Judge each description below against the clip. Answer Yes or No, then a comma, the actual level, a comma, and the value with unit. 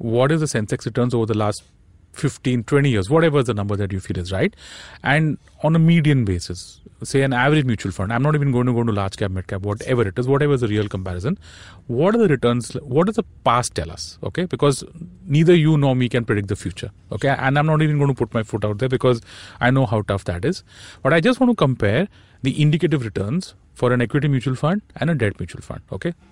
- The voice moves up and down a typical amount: No, wide, 6.1 semitones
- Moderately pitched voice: No, low, 125 Hz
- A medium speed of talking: No, fast, 245 wpm